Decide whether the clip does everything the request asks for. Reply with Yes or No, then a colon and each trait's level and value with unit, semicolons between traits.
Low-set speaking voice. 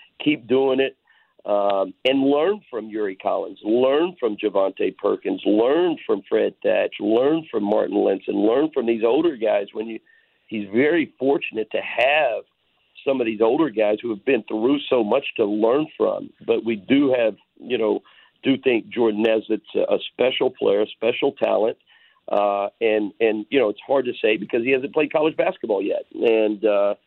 Yes: low, 130 Hz